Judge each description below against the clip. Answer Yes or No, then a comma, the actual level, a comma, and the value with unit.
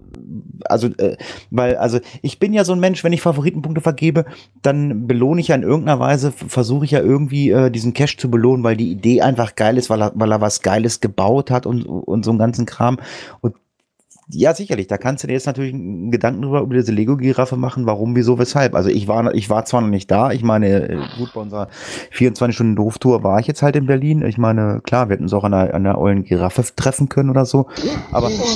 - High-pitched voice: No, low, 125 Hz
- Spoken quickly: Yes, fast, 225 wpm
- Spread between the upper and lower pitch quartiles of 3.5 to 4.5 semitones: Yes, average, 3.9 semitones